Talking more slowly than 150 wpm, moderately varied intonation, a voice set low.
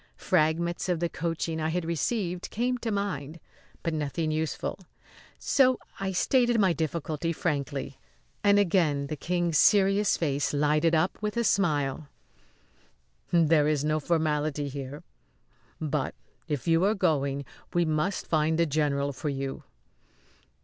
No: average, 140 wpm; average, 3.3 semitones; medium, 160 Hz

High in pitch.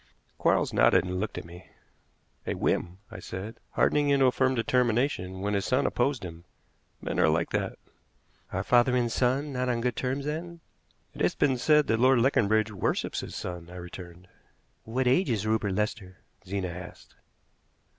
No: low, 115 Hz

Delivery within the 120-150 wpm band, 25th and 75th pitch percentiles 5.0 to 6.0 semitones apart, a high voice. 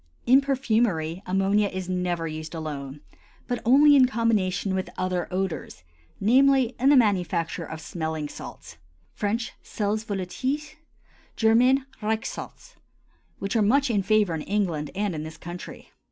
Yes: average, 140 wpm; wide, 5.4 semitones; high, 200 Hz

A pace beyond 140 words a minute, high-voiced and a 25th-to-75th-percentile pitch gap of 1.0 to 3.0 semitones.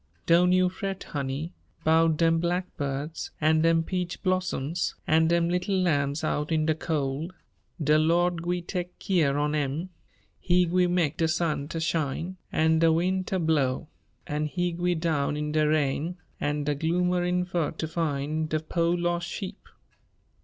No: average, 160 wpm; medium, 165 Hz; narrow, 2.6 semitones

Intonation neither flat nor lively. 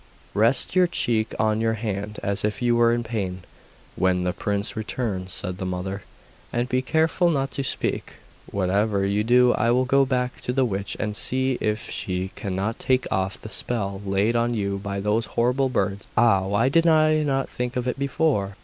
Yes: average, 4.3 semitones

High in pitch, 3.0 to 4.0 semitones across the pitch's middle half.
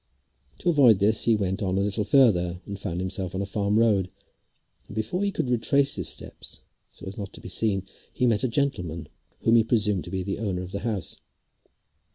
No: low, 105 Hz; average, 3.3 semitones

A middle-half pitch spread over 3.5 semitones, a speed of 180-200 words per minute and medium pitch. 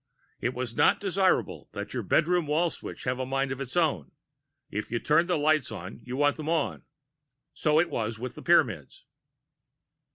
Yes: average, 4.4 semitones; average, 185 wpm; medium, 145 Hz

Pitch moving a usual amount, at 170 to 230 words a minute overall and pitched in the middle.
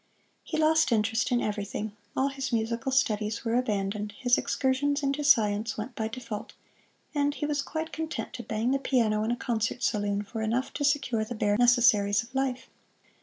No: average, 3.9 semitones; average, 180 wpm; high, 235 Hz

